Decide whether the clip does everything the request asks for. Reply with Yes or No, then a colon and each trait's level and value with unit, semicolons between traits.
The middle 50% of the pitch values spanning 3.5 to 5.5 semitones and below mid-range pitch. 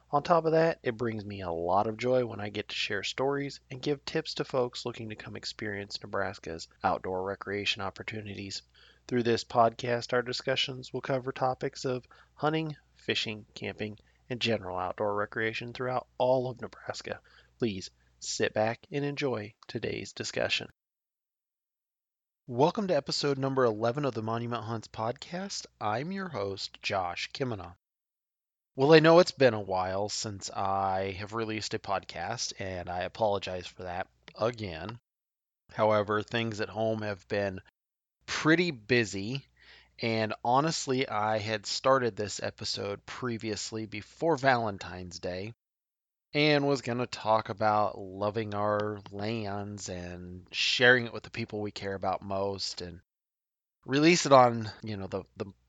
Yes: average, 4.2 semitones; low, 110 Hz